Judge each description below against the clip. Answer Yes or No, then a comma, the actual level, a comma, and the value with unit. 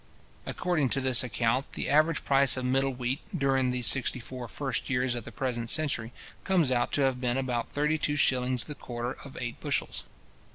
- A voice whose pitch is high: No, low, 130 Hz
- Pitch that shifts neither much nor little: No, narrow, 2.1 semitones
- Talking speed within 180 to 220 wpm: Yes, average, 195 wpm